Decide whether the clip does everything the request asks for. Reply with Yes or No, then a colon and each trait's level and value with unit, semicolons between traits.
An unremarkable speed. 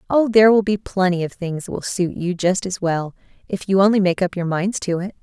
No: fast, 265 wpm